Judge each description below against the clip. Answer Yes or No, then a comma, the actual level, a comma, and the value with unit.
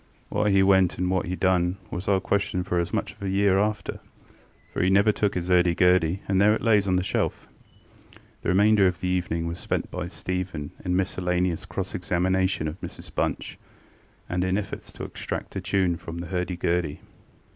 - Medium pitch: No, very low, 90 Hz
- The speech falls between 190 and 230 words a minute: Yes, average, 200 wpm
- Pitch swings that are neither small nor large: No, narrow, 1.6 semitones